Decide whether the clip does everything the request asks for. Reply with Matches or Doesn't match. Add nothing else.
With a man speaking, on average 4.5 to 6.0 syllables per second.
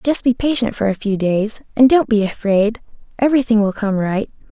Doesn't match